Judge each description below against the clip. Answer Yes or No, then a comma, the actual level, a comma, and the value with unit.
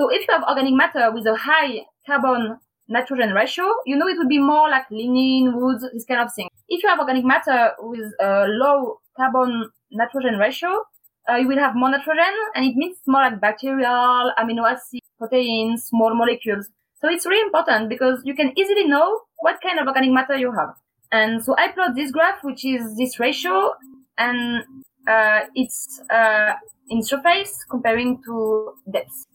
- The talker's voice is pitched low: No, very high, 260 Hz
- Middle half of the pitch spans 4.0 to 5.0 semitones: Yes, average, 4.3 semitones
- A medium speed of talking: Yes, average, 180 wpm